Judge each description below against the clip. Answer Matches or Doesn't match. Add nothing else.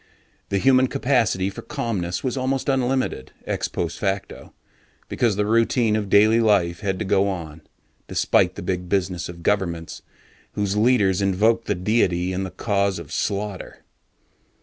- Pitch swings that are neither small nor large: Matches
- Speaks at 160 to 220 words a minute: Doesn't match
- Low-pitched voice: Matches